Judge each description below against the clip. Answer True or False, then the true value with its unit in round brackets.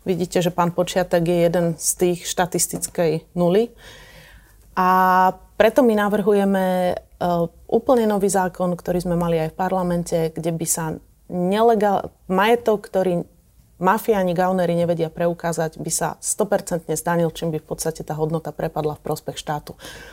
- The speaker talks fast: False (140 wpm)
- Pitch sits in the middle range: True (180 Hz)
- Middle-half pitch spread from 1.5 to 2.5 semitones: True (2.1 semitones)